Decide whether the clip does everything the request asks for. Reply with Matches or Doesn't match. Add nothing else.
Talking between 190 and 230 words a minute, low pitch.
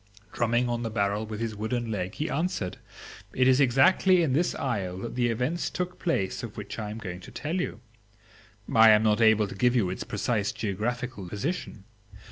Matches